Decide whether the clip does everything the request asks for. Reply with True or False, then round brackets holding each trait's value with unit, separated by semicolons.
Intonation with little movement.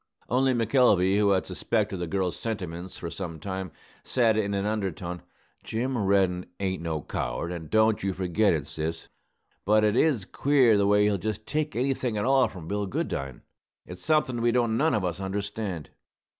False (3.9 semitones)